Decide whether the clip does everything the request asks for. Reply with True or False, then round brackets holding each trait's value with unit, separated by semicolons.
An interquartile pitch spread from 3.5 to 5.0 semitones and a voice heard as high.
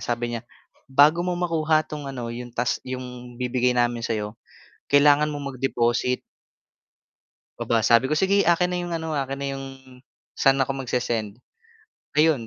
False (4.0 semitones; 135 Hz)